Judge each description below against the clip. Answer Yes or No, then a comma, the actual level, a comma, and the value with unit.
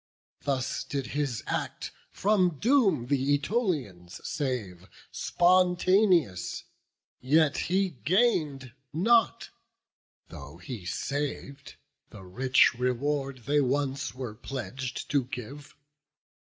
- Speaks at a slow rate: Yes, slow, 95 wpm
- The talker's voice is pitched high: No, medium, 140 Hz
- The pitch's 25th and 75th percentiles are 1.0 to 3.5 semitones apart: No, average, 5.3 semitones